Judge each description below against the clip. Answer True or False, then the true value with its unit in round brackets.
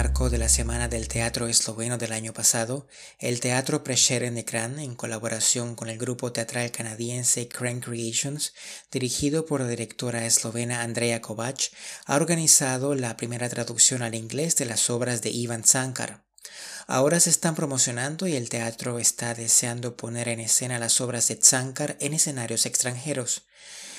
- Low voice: True (120 Hz)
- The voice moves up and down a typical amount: False (2.2 semitones)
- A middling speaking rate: True (160 wpm)